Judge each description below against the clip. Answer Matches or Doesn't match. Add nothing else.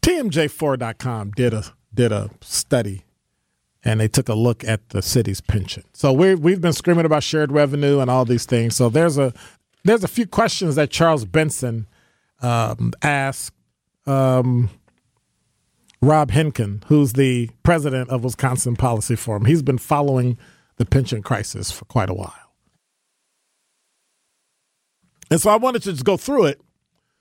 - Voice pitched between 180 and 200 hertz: Doesn't match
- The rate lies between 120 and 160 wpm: Matches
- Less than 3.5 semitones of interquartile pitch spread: Doesn't match